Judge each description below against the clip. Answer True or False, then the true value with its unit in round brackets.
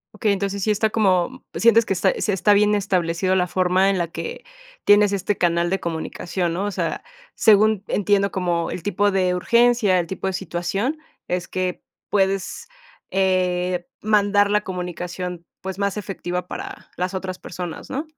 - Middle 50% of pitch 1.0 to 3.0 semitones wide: True (2.4 semitones)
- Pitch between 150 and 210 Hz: True (190 Hz)